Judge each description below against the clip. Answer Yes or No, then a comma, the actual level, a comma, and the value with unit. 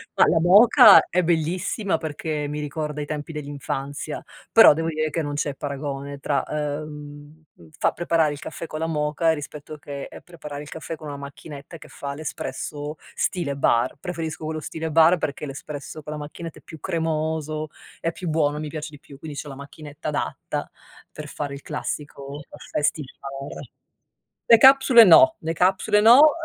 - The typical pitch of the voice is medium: Yes, medium, 150 Hz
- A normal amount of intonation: No, narrow, 2.0 semitones